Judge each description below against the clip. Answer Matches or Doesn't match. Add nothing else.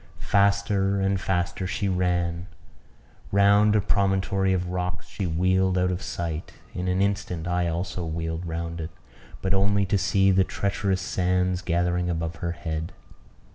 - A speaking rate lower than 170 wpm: Matches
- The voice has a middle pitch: Doesn't match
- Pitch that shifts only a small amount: Matches